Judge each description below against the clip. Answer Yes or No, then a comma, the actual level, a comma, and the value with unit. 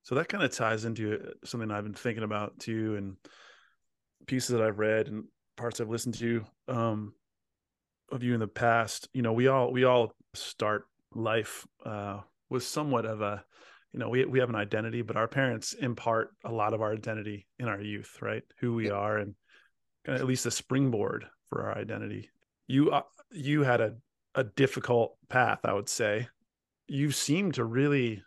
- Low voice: Yes, low, 115 Hz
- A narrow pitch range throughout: No, average, 3.2 semitones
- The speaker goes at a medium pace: Yes, average, 185 wpm